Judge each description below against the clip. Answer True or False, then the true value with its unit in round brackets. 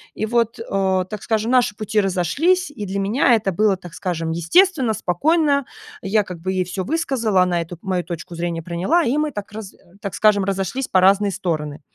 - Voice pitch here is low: False (200 Hz)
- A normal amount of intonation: True (4.5 semitones)